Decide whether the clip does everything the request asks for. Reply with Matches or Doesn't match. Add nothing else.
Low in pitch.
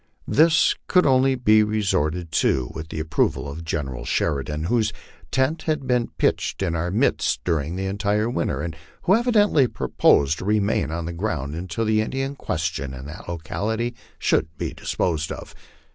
Matches